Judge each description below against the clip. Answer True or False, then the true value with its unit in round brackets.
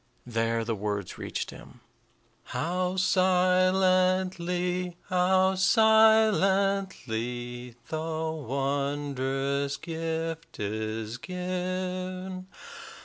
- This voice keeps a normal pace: False (65 wpm)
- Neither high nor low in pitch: True (175 Hz)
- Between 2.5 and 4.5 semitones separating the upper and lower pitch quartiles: False (5.5 semitones)